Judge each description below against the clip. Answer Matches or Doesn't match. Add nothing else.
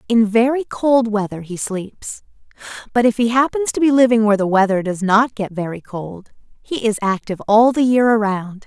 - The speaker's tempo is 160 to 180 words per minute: Doesn't match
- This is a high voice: Matches